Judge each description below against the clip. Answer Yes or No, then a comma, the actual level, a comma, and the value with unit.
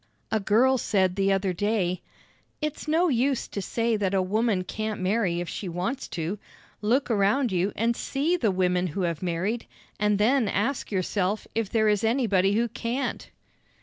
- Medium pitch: No, high, 210 Hz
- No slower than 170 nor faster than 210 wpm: Yes, average, 175 wpm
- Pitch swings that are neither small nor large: Yes, average, 3.9 semitones